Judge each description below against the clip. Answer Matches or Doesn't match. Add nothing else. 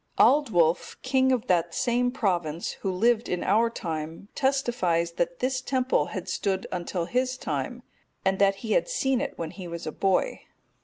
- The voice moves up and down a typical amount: Doesn't match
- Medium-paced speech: Matches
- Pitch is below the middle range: Doesn't match